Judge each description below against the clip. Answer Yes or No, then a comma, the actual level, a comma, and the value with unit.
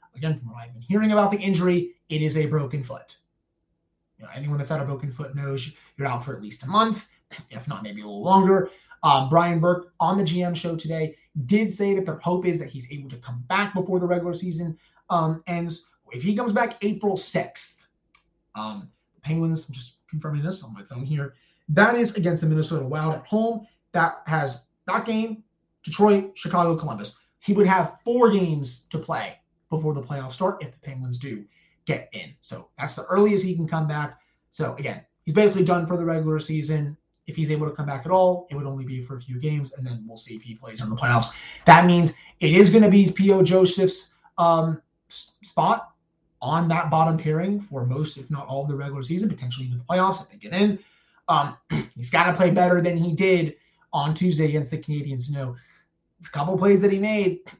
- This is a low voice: No, medium, 165 Hz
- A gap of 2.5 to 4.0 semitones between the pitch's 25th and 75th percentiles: No, average, 4.6 semitones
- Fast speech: Yes, fast, 220 wpm